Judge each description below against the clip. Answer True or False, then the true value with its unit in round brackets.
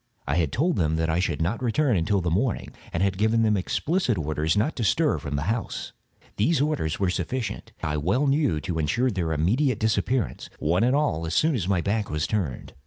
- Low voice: True (100 Hz)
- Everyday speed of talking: False (215 wpm)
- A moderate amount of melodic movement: False (7.4 semitones)